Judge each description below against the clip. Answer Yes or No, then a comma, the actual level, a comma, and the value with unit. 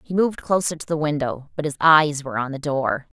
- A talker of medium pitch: Yes, medium, 150 Hz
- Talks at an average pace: No, fast, 245 wpm